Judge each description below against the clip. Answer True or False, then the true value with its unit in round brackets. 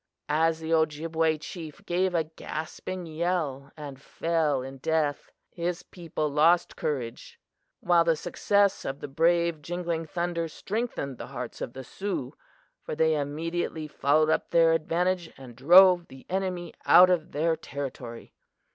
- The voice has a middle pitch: True (160 Hz)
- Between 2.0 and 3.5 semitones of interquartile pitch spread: True (2.8 semitones)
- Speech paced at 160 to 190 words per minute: False (145 wpm)